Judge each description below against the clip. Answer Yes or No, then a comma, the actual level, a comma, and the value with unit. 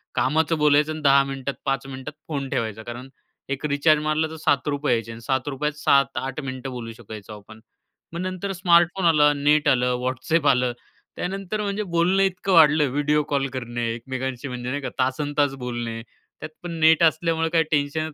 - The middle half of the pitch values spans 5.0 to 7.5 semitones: No, average, 3.6 semitones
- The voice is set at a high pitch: No, medium, 145 Hz